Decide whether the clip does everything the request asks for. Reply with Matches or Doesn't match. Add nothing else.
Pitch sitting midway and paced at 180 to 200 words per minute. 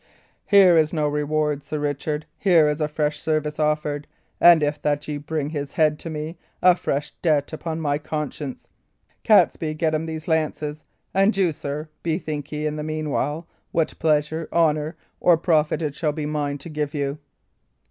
Doesn't match